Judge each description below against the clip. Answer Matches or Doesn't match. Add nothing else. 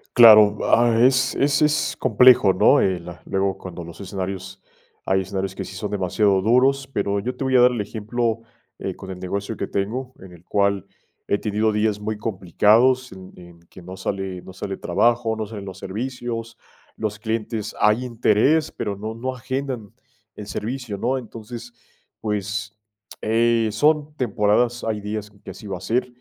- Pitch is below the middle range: Matches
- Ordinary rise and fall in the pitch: Matches